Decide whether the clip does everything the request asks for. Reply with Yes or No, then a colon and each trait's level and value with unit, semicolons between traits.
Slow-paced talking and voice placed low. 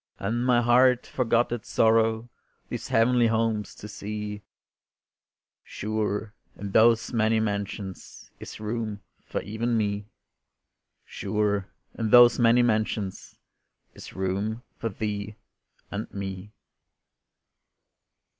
Yes: slow, 105 wpm; low, 110 Hz